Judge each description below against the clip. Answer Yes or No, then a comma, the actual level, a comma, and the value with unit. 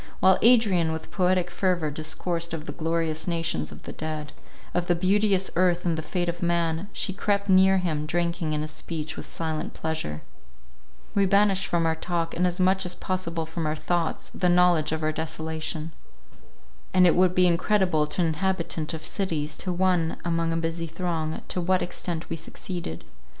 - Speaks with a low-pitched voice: No, medium, 170 Hz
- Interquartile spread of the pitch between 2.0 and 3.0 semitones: Yes, narrow, 2.4 semitones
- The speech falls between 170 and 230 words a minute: Yes, average, 185 wpm